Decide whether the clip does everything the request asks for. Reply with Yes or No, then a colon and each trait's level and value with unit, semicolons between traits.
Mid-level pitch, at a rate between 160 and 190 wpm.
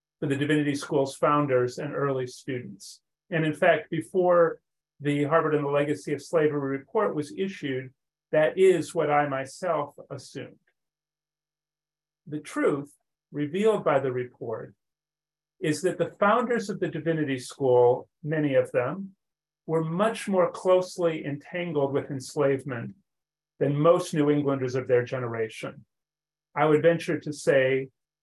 No: medium, 150 Hz; slow, 135 wpm